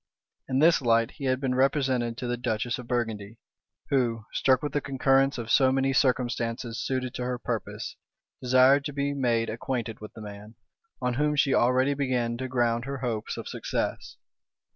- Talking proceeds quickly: No, average, 180 wpm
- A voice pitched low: Yes, low, 125 Hz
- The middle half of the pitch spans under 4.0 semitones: Yes, narrow, 2.4 semitones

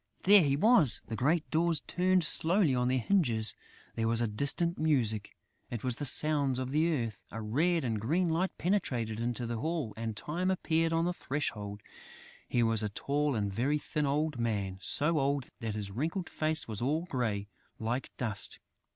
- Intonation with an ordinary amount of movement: No, wide, 6.3 semitones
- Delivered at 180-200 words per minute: Yes, average, 185 wpm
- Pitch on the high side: No, low, 135 Hz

